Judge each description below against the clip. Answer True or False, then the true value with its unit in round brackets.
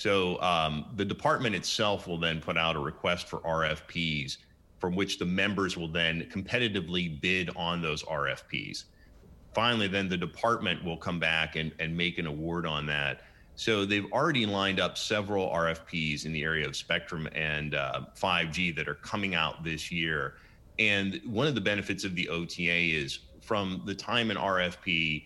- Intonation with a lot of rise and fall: False (3.4 semitones)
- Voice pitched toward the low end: True (85 Hz)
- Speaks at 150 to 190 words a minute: True (175 wpm)